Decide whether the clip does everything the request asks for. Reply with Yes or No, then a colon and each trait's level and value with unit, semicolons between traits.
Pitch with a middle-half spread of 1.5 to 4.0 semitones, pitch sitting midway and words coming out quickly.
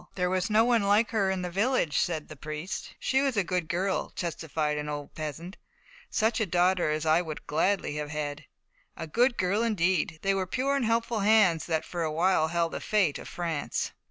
No: average, 5.0 semitones; medium, 180 Hz; fast, 210 wpm